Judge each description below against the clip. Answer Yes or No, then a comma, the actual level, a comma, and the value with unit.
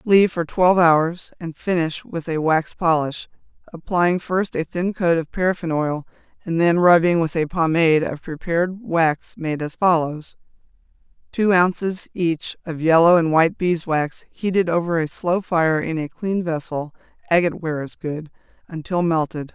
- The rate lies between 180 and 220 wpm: No, average, 165 wpm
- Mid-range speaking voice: Yes, medium, 165 Hz